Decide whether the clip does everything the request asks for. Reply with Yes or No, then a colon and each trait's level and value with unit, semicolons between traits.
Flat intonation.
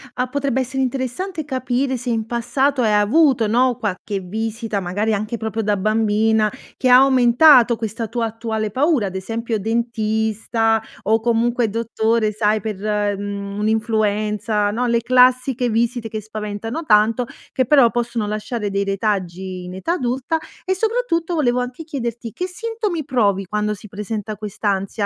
No: average, 3.1 semitones